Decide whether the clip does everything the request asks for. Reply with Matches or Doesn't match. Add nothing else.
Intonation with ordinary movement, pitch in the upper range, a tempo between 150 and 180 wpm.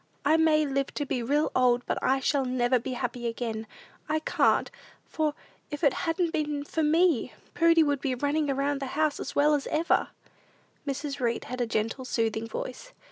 Doesn't match